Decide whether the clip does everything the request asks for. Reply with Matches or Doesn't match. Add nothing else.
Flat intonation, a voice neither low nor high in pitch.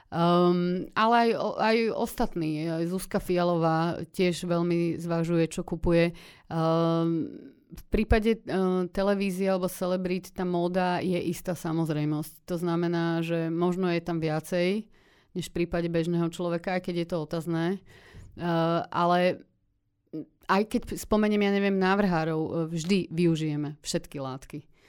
Matches